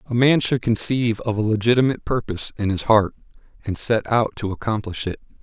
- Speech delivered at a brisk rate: No, average, 190 wpm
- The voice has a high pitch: No, low, 115 Hz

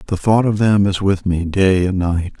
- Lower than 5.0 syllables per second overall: Yes, 4.7 syllables/s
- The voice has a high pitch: No, very low, 95 Hz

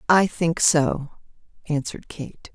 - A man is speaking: No, female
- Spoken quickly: No, slow, 120 wpm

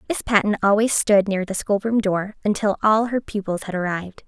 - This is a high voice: Yes, high, 205 Hz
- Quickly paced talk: No, average, 195 wpm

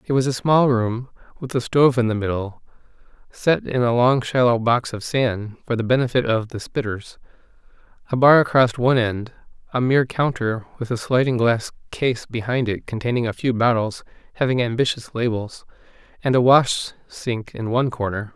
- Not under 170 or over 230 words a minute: Yes, average, 175 wpm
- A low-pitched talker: Yes, low, 120 Hz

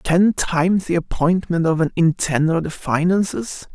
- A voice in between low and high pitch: Yes, medium, 170 Hz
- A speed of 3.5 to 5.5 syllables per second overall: Yes, 4.7 syllables/s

